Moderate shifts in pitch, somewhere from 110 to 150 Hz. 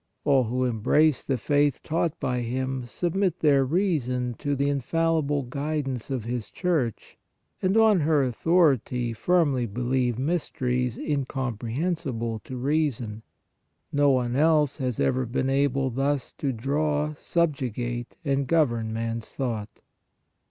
Yes: average, 3.7 semitones; low, 135 Hz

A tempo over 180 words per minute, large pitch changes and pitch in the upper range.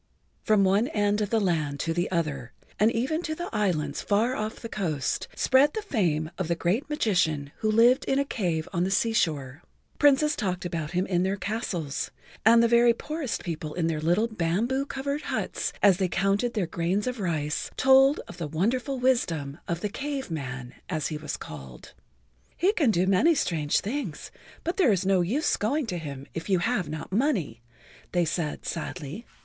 Yes: average, 190 wpm; wide, 6.7 semitones; high, 195 Hz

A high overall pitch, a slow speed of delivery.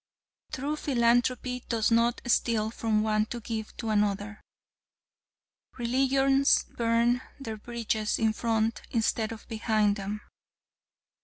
Yes: high, 230 Hz; slow, 110 wpm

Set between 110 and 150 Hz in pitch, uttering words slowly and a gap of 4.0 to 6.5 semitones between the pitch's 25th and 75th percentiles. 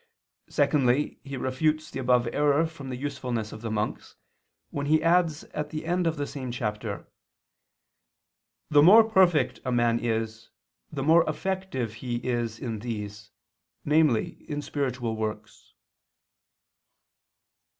Yes: low, 135 Hz; slow, 130 wpm; average, 4.9 semitones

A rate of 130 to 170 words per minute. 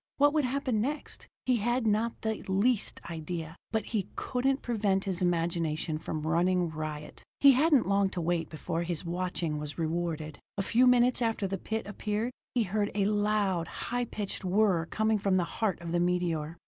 No: average, 180 wpm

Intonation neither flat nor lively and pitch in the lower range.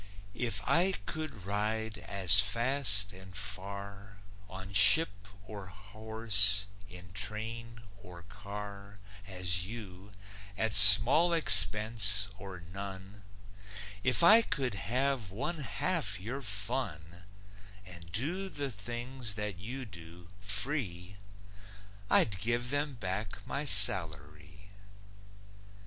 Yes: average, 3.7 semitones; low, 105 Hz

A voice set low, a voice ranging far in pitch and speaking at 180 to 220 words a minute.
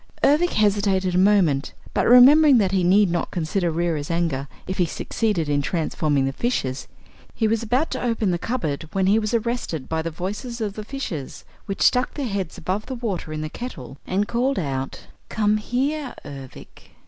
No: high, 195 Hz; wide, 6.5 semitones; average, 185 wpm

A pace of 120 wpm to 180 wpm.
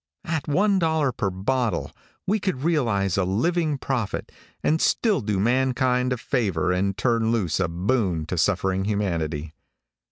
Yes: average, 150 wpm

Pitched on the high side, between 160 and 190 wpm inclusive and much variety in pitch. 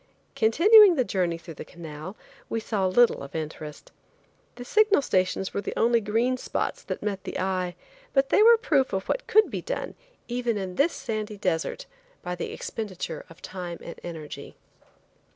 Yes: high, 205 Hz; average, 170 wpm; wide, 6.1 semitones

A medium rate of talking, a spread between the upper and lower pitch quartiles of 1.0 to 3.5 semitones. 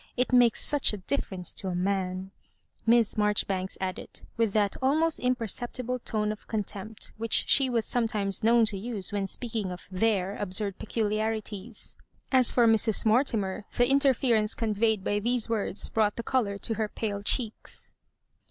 Yes: average, 160 wpm; average, 2.8 semitones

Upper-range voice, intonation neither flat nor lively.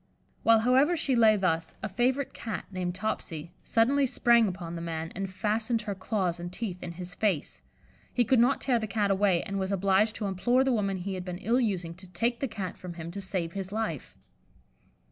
Yes: high, 200 Hz; average, 4.1 semitones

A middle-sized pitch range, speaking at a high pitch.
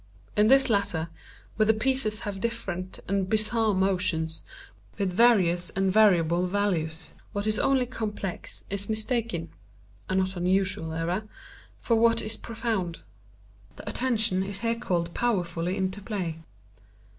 Yes: average, 3.5 semitones; high, 200 Hz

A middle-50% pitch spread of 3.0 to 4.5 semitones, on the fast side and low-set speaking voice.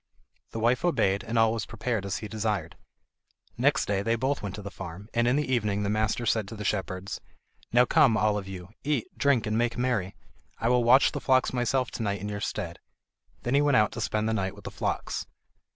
Yes: average, 3.3 semitones; fast, 230 wpm; low, 110 Hz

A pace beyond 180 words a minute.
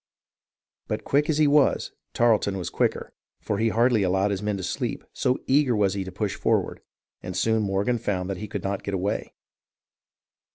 Yes: average, 190 wpm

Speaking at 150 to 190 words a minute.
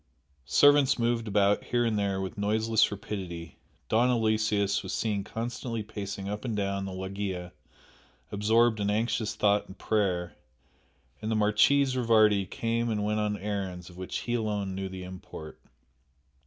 Yes: average, 155 wpm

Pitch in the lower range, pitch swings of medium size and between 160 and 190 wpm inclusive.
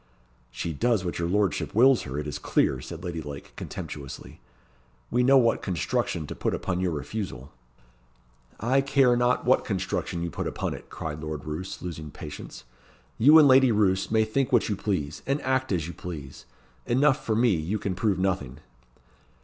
No: very low, 95 Hz; wide, 7.5 semitones; average, 180 wpm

